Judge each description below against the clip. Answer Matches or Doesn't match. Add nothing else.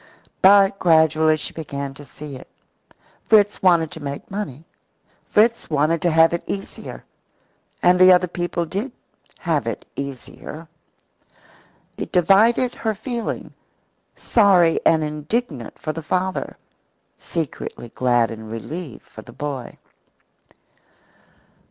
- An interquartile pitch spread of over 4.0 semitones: Matches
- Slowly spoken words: Matches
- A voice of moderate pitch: Matches